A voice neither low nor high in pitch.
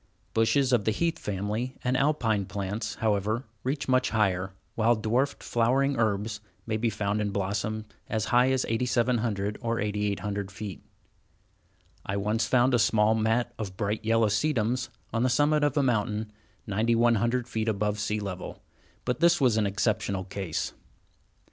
No: low, 110 Hz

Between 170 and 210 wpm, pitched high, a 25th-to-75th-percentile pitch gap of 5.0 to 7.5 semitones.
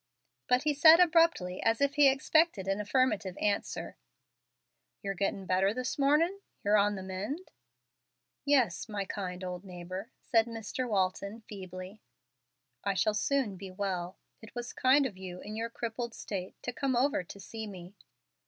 No: average, 160 wpm; high, 210 Hz; average, 5.3 semitones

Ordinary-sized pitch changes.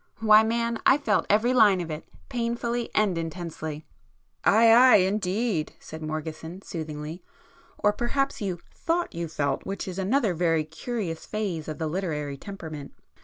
No: wide, 6.0 semitones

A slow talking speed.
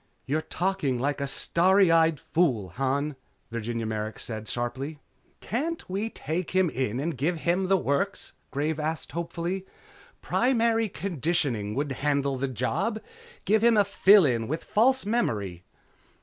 No: average, 145 wpm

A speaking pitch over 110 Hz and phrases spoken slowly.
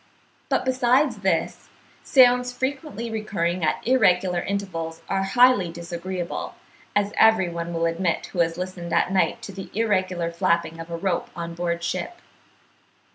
No: medium, 185 Hz; average, 145 wpm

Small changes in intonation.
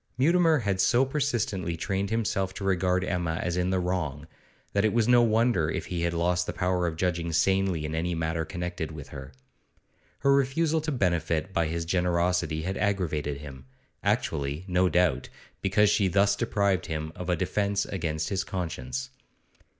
No: average, 3.6 semitones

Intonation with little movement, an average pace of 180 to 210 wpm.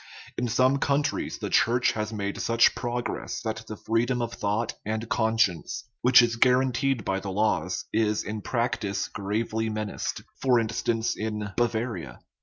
No: narrow, 2.2 semitones; average, 150 wpm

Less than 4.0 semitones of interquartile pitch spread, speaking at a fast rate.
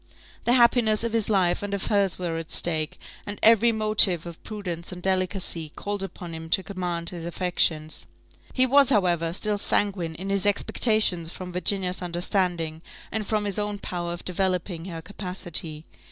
No: average, 3.2 semitones; average, 170 wpm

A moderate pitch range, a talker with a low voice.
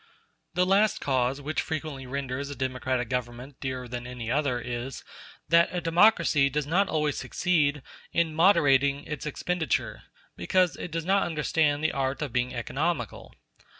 No: average, 4.2 semitones; medium, 145 Hz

